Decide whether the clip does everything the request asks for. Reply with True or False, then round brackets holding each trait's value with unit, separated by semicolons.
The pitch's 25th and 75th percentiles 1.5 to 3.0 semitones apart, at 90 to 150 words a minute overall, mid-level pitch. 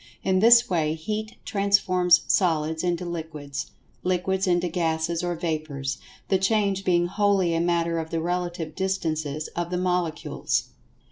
True (2.7 semitones; 140 wpm; 175 Hz)